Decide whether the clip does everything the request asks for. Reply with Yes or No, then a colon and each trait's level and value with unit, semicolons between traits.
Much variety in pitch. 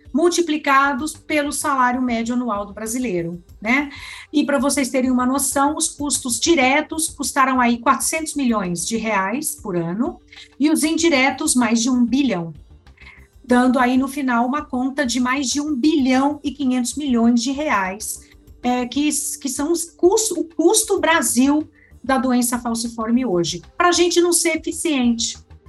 No: average, 3.9 semitones